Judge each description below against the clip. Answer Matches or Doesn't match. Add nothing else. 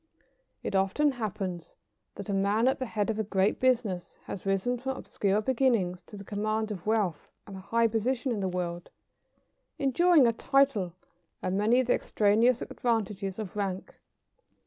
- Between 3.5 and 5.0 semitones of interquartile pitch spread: Matches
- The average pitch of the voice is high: Matches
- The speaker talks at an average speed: Matches